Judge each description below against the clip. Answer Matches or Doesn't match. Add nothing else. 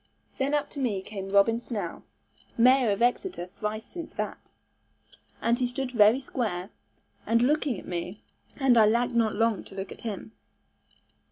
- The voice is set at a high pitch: Matches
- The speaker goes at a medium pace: Matches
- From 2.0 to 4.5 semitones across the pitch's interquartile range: Matches